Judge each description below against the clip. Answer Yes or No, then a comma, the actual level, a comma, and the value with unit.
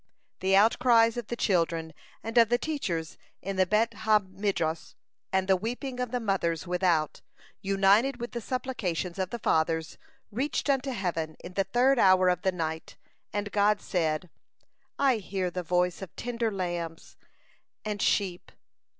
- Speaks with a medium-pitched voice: No, high, 195 Hz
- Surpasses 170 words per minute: No, average, 160 wpm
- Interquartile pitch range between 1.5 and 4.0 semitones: No, average, 4.4 semitones